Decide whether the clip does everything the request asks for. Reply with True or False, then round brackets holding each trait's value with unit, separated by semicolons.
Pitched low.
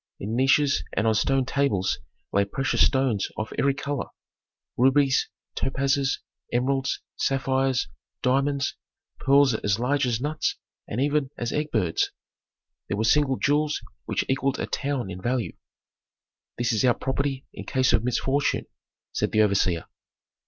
True (130 Hz)